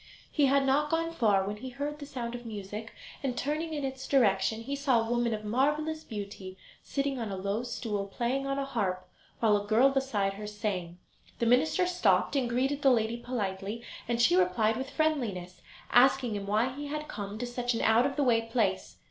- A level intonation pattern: No, average, 4.8 semitones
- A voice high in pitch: Yes, high, 240 Hz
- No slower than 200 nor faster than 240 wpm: Yes, fast, 205 wpm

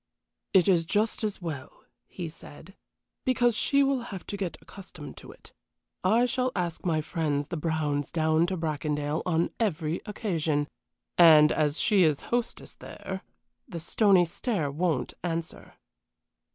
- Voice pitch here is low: No, medium, 170 Hz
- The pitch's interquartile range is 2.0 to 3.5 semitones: No, average, 4.4 semitones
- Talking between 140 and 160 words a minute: Yes, average, 145 wpm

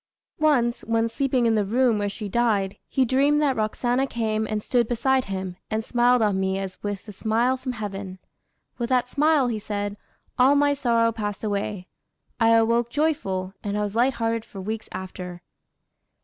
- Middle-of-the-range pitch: No, high, 225 Hz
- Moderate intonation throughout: Yes, average, 3.5 semitones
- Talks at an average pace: Yes, average, 175 wpm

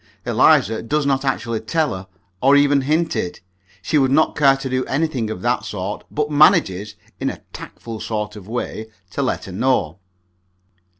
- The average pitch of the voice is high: No, low, 130 Hz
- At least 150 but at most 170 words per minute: No, average, 180 wpm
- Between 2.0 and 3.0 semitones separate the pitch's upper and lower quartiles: No, average, 5.2 semitones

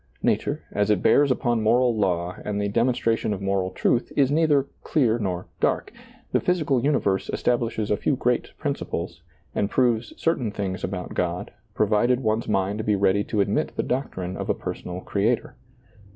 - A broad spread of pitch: No, average, 4.2 semitones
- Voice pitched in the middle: No, low, 110 Hz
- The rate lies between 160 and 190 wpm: Yes, average, 170 wpm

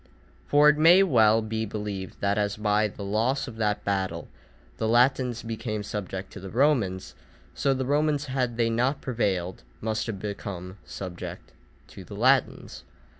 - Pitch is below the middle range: Yes, low, 110 Hz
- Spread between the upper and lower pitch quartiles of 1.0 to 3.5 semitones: No, average, 4.2 semitones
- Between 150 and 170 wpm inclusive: Yes, average, 160 wpm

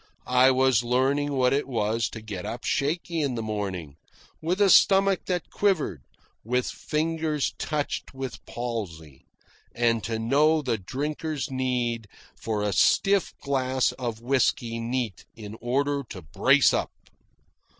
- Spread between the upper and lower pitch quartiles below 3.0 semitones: No, average, 4.3 semitones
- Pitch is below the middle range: Yes, low, 125 Hz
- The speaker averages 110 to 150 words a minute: Yes, average, 140 wpm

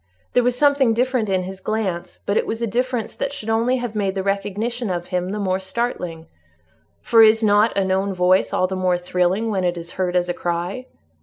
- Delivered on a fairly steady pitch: No, average, 3.9 semitones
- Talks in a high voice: Yes, high, 200 Hz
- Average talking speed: No, fast, 220 wpm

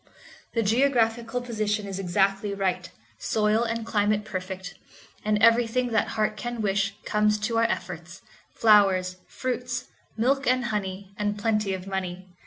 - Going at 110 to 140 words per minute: Yes, slow, 135 wpm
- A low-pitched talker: No, high, 210 Hz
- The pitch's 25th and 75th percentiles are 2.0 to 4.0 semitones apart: Yes, average, 2.9 semitones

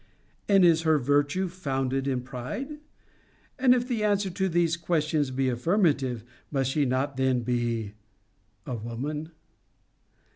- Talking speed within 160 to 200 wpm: No, slow, 135 wpm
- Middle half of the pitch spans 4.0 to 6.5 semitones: Yes, wide, 5.5 semitones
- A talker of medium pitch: Yes, medium, 145 Hz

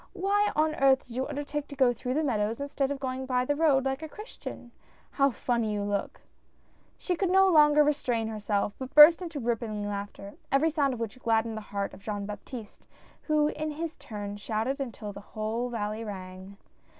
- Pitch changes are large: Yes, wide, 5.7 semitones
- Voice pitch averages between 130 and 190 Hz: No, very high, 250 Hz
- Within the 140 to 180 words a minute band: No, average, 200 wpm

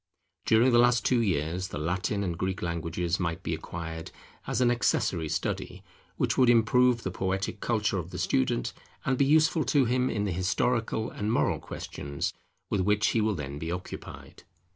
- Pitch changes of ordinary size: No, wide, 5.8 semitones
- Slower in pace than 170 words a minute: No, average, 180 wpm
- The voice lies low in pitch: Yes, low, 100 Hz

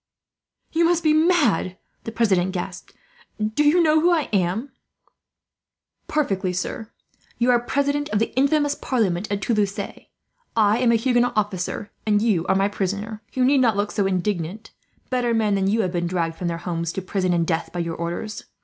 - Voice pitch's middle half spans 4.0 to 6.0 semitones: Yes, wide, 5.4 semitones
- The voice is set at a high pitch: Yes, high, 210 Hz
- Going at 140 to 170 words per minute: No, average, 185 wpm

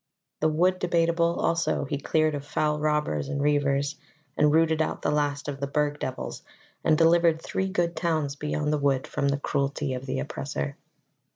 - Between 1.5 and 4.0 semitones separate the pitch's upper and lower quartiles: Yes, narrow, 2.6 semitones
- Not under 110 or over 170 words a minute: No, average, 180 wpm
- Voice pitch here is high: No, medium, 150 Hz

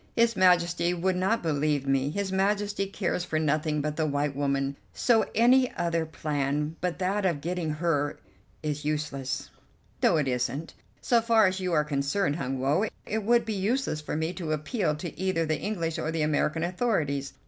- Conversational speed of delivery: Yes, average, 180 wpm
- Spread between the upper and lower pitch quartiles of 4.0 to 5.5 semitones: Yes, average, 4.3 semitones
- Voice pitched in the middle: Yes, medium, 165 Hz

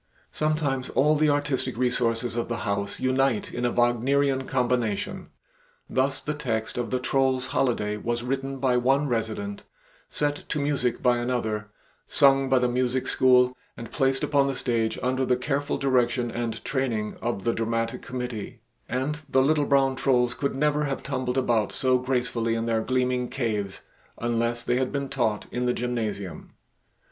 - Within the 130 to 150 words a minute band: No, average, 165 wpm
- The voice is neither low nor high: No, low, 125 Hz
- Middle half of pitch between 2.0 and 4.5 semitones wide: Yes, narrow, 2.4 semitones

